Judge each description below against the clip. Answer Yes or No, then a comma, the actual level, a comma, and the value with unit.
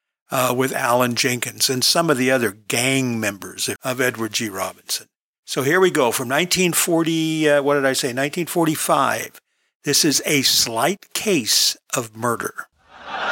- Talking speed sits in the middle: Yes, average, 155 wpm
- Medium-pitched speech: No, low, 130 Hz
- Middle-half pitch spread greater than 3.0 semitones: Yes, average, 4.9 semitones